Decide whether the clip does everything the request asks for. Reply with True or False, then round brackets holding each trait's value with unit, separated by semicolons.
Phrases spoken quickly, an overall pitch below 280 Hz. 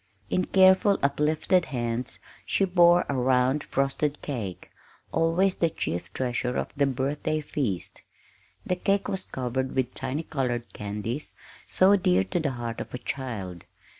False (150 wpm; 135 Hz)